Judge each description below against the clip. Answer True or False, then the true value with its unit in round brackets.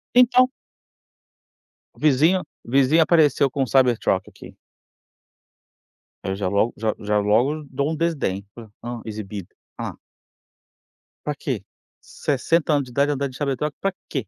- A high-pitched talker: False (135 Hz)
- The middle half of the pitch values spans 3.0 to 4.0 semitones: False (5.6 semitones)